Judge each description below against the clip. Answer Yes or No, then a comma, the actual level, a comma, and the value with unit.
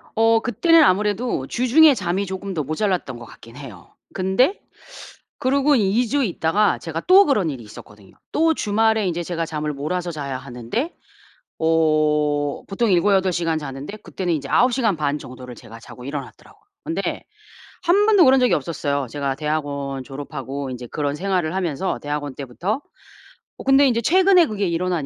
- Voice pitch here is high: No, medium, 175 Hz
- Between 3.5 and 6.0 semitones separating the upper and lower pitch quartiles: No, wide, 7.7 semitones